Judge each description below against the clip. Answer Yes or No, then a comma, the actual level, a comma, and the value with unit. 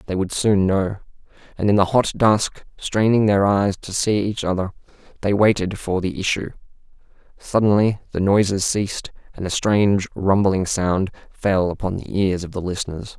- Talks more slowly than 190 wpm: Yes, average, 170 wpm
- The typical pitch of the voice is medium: No, low, 100 Hz